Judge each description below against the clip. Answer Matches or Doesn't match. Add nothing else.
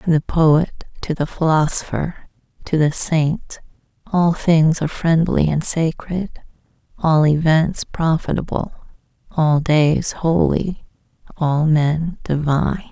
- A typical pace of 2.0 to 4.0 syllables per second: Matches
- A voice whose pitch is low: Doesn't match